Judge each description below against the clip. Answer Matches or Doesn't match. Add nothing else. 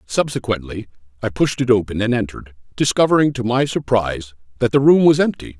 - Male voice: Matches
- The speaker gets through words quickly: Doesn't match